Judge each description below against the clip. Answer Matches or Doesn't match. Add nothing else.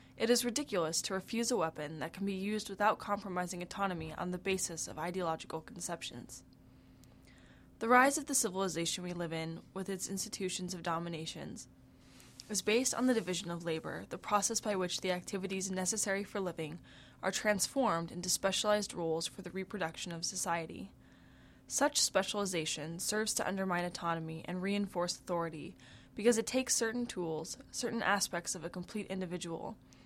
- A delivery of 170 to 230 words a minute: Doesn't match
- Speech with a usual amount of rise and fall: Matches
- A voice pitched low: Doesn't match